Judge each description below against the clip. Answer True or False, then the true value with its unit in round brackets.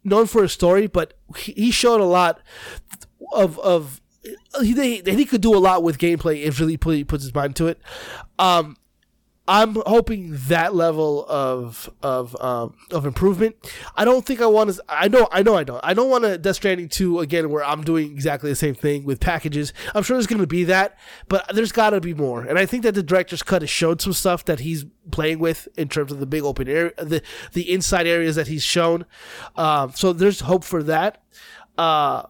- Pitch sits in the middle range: True (170 Hz)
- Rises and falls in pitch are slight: False (4.7 semitones)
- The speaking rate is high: True (220 wpm)